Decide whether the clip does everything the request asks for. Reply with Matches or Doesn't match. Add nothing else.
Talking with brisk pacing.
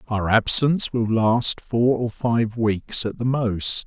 Doesn't match